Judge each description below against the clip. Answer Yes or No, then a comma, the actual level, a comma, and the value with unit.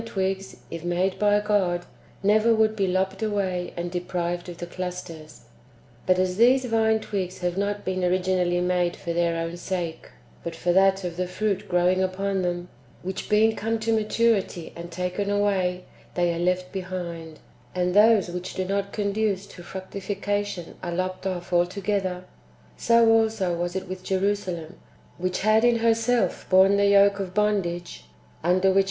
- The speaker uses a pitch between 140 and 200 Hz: Yes, medium, 185 Hz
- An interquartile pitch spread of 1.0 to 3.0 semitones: Yes, narrow, 2.5 semitones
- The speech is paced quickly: No, average, 165 wpm